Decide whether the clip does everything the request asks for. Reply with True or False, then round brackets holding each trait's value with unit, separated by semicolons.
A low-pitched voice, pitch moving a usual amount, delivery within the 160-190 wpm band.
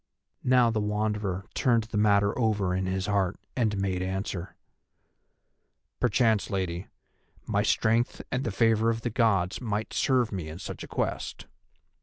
False (105 Hz; 3.1 semitones; 150 wpm)